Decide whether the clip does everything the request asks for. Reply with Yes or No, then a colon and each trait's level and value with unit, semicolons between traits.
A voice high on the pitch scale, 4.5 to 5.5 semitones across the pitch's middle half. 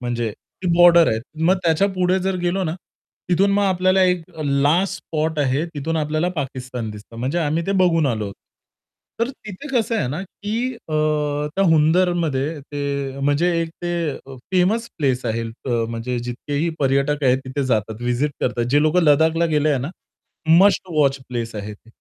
No: medium, 150 Hz; average, 5.1 semitones